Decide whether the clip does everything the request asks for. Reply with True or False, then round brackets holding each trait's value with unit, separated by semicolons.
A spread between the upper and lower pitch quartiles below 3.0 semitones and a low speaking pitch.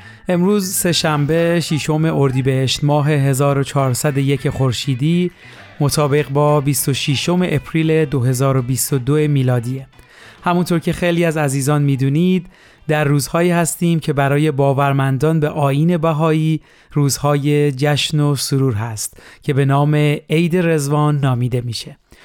False (2.6 semitones; 145 Hz)